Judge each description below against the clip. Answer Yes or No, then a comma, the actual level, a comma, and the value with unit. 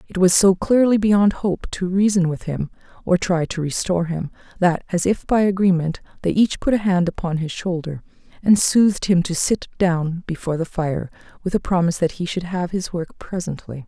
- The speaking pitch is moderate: Yes, medium, 180 Hz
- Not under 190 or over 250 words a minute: Yes, average, 195 wpm